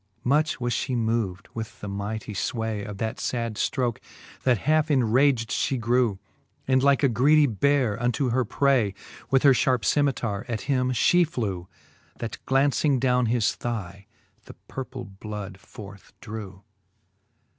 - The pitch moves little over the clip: No, average, 4.0 semitones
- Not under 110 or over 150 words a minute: Yes, average, 145 wpm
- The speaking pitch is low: Yes, low, 120 Hz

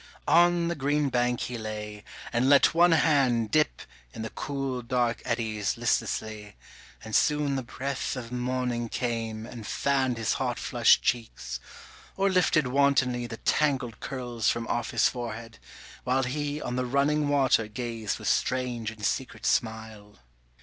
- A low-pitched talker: Yes, low, 125 Hz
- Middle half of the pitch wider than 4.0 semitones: No, average, 3.5 semitones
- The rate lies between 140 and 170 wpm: Yes, average, 150 wpm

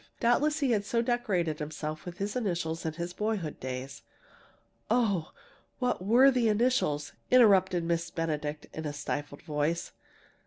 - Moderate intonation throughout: No, wide, 7.0 semitones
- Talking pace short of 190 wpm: Yes, average, 150 wpm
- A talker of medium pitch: Yes, medium, 175 Hz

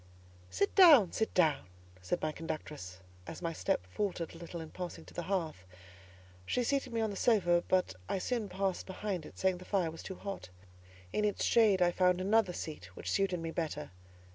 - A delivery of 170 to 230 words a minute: Yes, average, 190 wpm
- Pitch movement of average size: Yes, average, 3.6 semitones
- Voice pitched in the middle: Yes, medium, 180 Hz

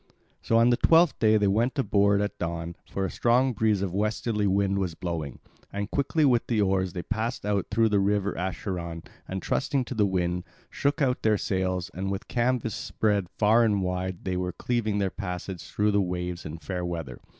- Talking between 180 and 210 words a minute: Yes, average, 200 wpm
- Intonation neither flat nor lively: Yes, average, 3.5 semitones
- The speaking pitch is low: Yes, low, 100 Hz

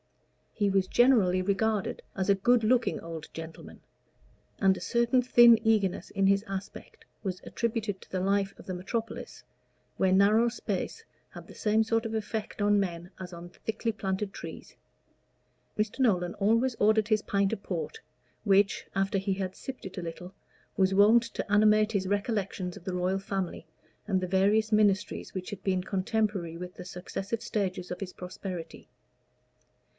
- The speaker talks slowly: No, average, 165 wpm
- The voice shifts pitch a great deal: No, average, 2.8 semitones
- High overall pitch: Yes, high, 200 Hz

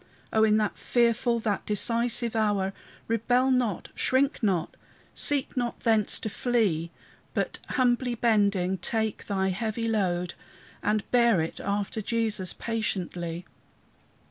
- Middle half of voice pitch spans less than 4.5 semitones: Yes, average, 3.3 semitones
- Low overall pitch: No, high, 220 Hz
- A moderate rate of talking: No, slow, 120 wpm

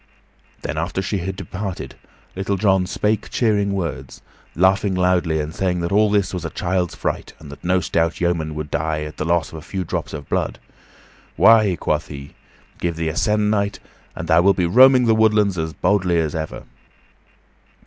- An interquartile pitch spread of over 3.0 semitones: Yes, average, 3.7 semitones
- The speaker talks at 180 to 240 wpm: Yes, average, 185 wpm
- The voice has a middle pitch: No, very low, 90 Hz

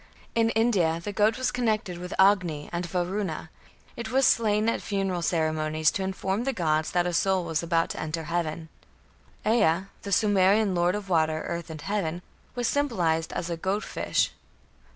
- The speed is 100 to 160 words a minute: No, average, 175 wpm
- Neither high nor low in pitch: Yes, medium, 180 Hz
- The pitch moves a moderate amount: Yes, average, 4.1 semitones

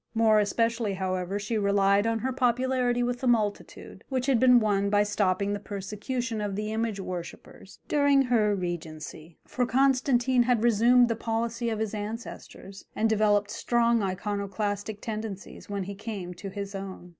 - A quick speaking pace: No, average, 160 wpm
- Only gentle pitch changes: No, average, 3.1 semitones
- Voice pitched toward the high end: Yes, high, 215 Hz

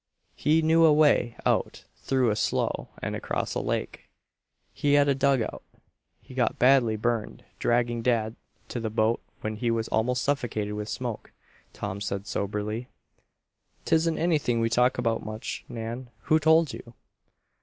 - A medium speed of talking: Yes, average, 155 wpm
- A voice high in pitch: No, low, 120 Hz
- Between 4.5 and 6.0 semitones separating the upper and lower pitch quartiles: No, average, 4.0 semitones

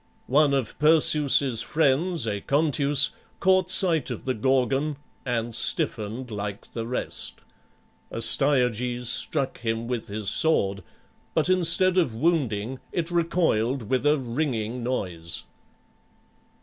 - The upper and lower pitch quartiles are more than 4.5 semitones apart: Yes, average, 5.2 semitones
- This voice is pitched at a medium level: No, low, 130 Hz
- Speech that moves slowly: Yes, slow, 110 wpm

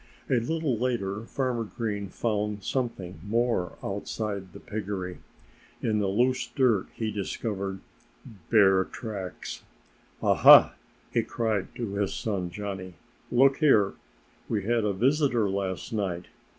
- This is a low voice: Yes, low, 105 Hz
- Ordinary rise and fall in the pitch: Yes, average, 3.4 semitones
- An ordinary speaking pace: No, slow, 125 wpm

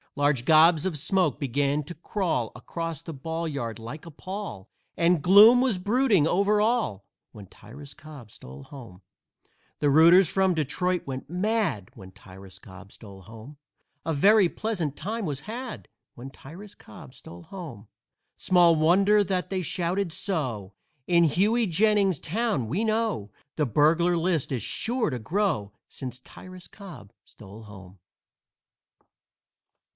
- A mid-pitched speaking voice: Yes, medium, 160 Hz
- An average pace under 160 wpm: Yes, average, 140 wpm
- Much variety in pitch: Yes, wide, 7.7 semitones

